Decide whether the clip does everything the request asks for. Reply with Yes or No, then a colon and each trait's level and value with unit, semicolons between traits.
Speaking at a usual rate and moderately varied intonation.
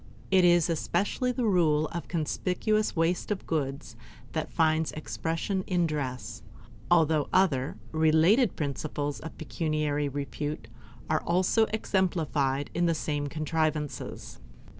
No: slow, 125 wpm; average, 3.1 semitones